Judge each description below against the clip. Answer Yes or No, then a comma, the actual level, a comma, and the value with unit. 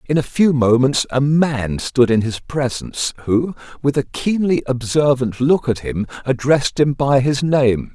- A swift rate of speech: No, average, 175 wpm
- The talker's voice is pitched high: No, low, 135 Hz